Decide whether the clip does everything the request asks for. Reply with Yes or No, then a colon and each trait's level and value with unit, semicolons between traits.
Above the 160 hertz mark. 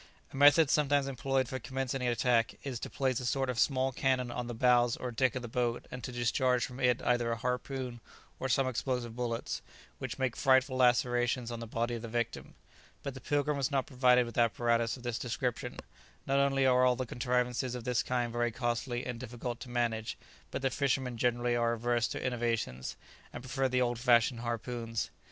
No: low, 125 Hz